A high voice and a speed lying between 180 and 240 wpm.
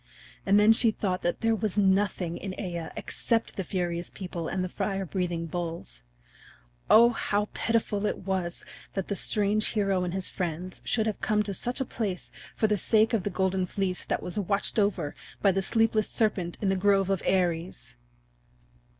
Yes: high, 195 Hz; average, 185 wpm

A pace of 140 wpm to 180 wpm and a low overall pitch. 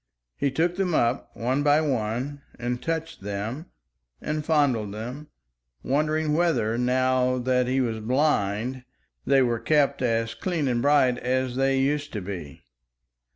Yes: average, 145 wpm; low, 130 Hz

